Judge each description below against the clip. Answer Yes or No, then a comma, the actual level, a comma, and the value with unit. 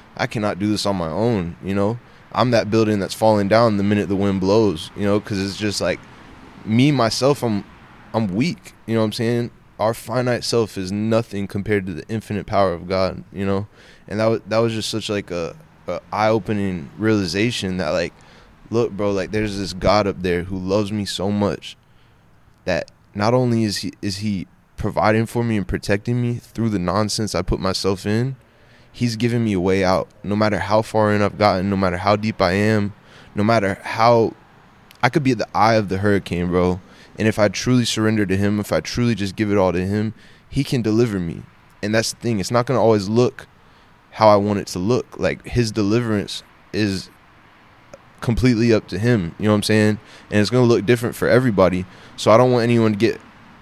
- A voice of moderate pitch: No, low, 105 Hz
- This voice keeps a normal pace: No, fast, 215 wpm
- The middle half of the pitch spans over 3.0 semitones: No, narrow, 2.5 semitones